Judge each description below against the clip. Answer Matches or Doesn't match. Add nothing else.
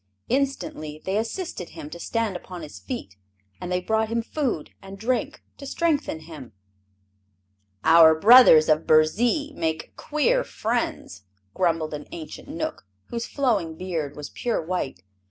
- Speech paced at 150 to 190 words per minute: Doesn't match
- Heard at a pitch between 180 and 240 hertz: Matches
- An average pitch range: Doesn't match